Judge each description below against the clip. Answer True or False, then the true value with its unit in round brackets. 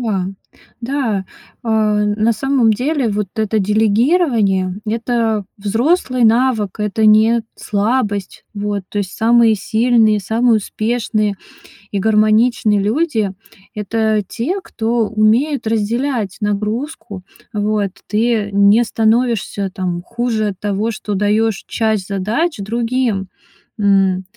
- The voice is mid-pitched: False (220 Hz)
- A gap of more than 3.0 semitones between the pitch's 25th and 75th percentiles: False (2.5 semitones)